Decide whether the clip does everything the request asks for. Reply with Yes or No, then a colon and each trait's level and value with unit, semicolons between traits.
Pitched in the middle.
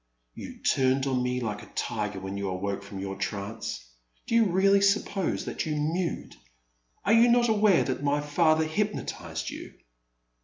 Yes: medium, 145 Hz